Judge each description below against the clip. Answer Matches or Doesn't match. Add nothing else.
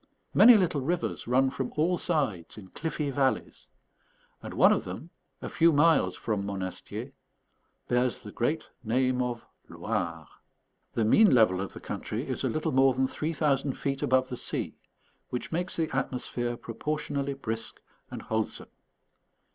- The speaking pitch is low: Matches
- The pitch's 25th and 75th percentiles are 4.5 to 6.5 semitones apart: Matches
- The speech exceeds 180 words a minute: Doesn't match